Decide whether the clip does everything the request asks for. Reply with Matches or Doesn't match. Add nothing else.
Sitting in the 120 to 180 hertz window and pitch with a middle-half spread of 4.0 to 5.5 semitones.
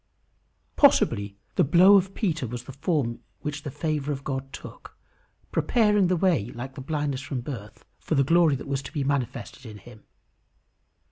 Matches